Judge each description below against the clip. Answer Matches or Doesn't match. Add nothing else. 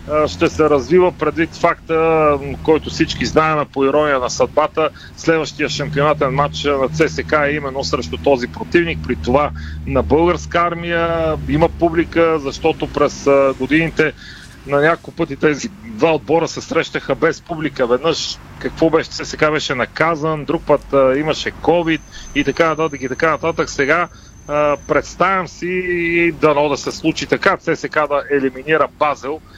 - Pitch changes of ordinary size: Doesn't match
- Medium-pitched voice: Matches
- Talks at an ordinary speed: Matches